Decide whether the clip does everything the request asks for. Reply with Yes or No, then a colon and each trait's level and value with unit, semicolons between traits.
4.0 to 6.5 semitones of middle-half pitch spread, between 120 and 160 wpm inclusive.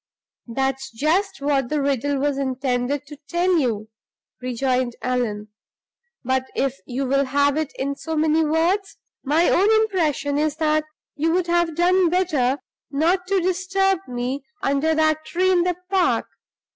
Yes: average, 4.5 semitones; average, 150 wpm